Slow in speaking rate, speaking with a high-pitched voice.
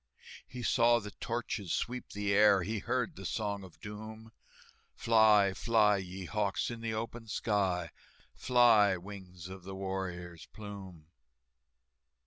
No: slow, 130 wpm; low, 105 Hz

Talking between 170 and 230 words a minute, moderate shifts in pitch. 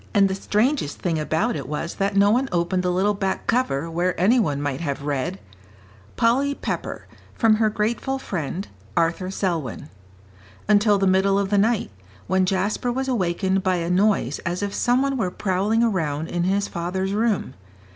Yes: average, 175 wpm; average, 4.0 semitones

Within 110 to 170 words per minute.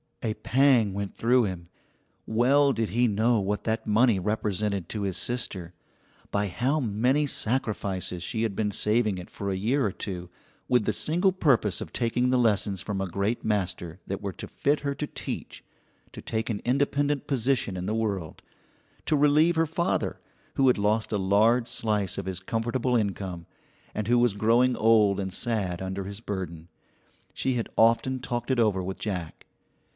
No: average, 180 wpm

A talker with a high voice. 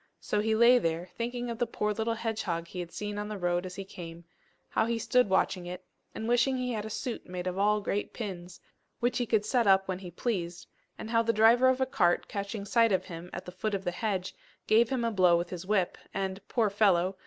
Yes: high, 205 Hz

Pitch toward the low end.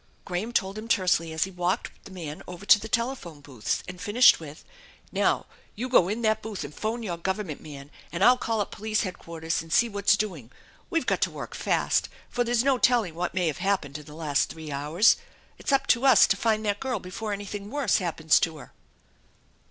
No: high, 195 Hz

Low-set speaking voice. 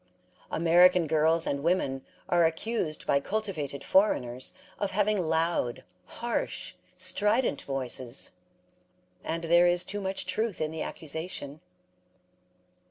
No: medium, 165 Hz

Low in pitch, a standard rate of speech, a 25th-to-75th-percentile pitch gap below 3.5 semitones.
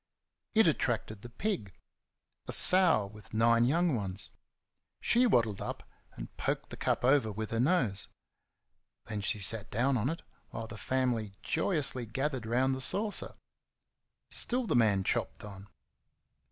No: low, 120 Hz; average, 145 wpm; average, 5.1 semitones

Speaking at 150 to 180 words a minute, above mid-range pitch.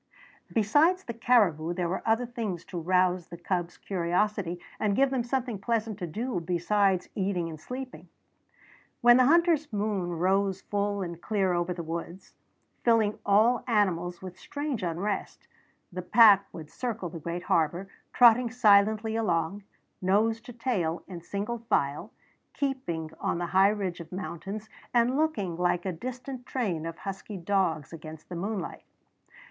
Yes: average, 155 wpm; high, 200 Hz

